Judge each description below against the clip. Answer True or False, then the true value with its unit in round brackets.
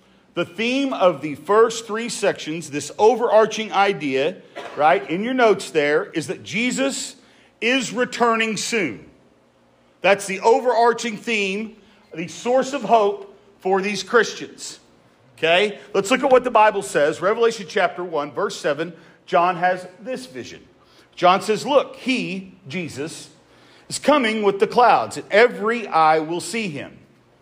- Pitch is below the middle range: False (200 Hz)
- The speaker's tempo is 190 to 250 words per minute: False (140 wpm)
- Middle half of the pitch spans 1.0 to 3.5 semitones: False (5.6 semitones)